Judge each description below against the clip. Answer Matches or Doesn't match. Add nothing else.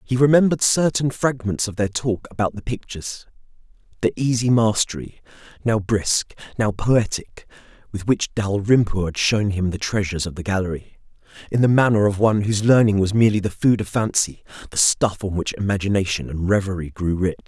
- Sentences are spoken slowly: Doesn't match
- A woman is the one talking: Doesn't match